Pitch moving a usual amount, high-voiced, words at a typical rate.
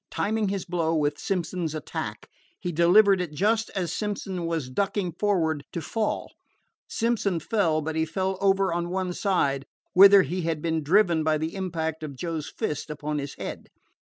No: average, 3.7 semitones; medium, 170 Hz; average, 170 wpm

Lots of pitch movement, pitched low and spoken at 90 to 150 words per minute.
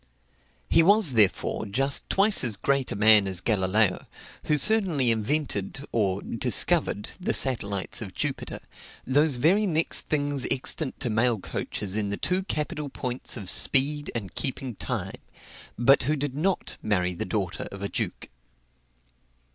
Yes: wide, 6.6 semitones; low, 125 Hz; average, 145 wpm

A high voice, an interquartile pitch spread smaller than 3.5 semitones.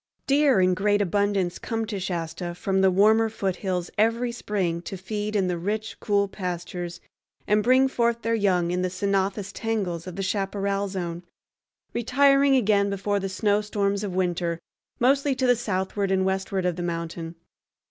Yes: high, 200 Hz; average, 3.0 semitones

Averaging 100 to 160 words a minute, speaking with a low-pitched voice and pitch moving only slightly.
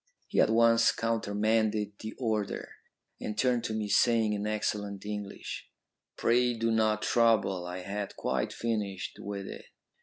Yes: average, 145 wpm; low, 110 Hz; narrow, 1.9 semitones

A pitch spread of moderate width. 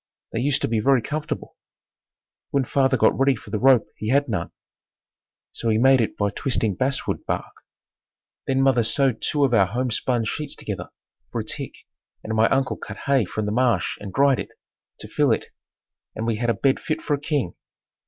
Yes: average, 3.7 semitones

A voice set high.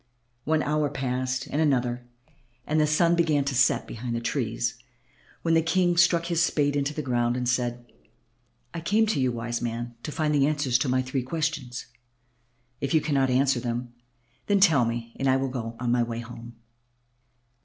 No: low, 135 Hz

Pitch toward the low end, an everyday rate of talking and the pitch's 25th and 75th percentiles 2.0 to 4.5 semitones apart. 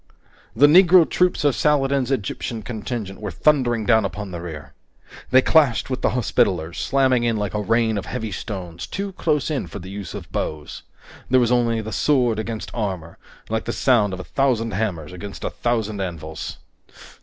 No: low, 110 Hz; average, 180 wpm; average, 5.0 semitones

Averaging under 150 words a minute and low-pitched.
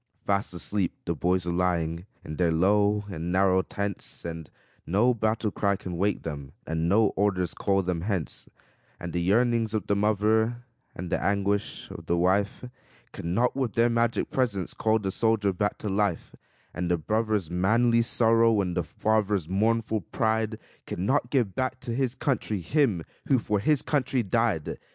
No: average, 175 wpm; low, 100 Hz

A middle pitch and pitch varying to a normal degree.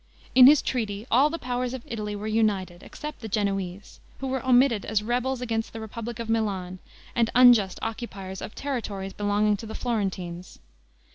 No: high, 220 Hz; average, 3.5 semitones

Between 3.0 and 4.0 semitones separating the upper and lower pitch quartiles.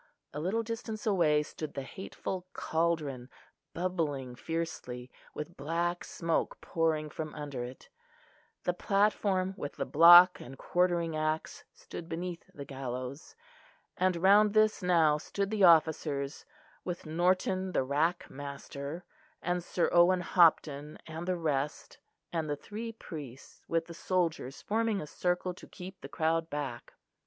Yes: average, 3.7 semitones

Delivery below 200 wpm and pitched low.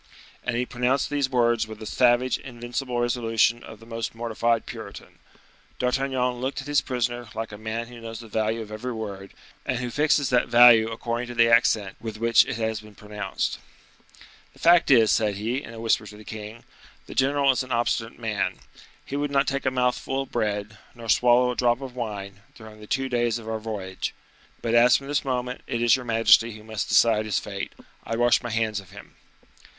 No: fast, 205 wpm; low, 115 Hz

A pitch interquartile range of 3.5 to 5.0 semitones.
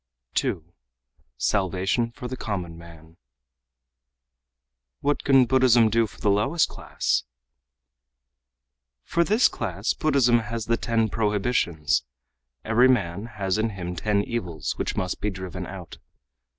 Yes: average, 4.5 semitones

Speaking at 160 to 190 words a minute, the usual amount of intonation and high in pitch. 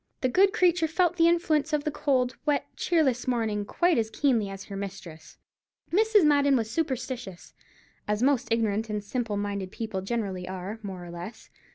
No: average, 175 wpm; wide, 6.7 semitones; high, 235 Hz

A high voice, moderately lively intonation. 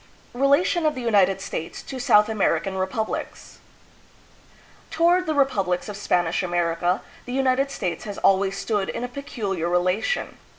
No: high, 210 Hz; wide, 6.5 semitones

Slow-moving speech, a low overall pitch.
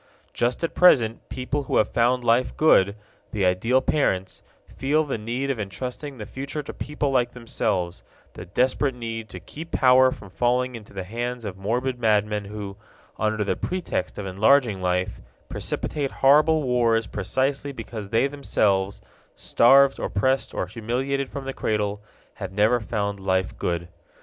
No: average, 155 wpm; low, 120 Hz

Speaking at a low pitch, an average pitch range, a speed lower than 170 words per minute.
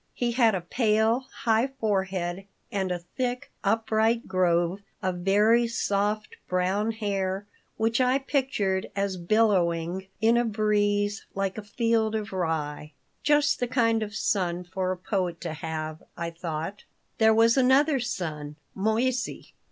No: high, 205 Hz; average, 3.8 semitones; average, 140 wpm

